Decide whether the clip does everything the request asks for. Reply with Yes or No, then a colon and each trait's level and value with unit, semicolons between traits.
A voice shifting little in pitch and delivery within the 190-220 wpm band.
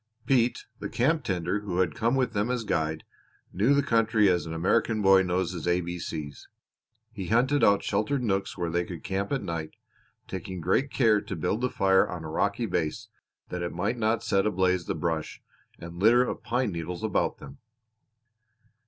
No: average, 4.7 semitones; average, 195 wpm